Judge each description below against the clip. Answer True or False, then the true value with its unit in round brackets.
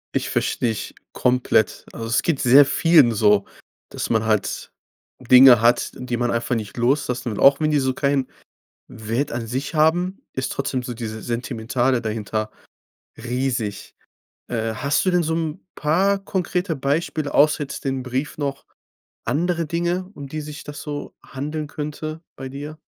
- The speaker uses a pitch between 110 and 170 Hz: True (135 Hz)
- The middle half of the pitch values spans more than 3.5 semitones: True (4.3 semitones)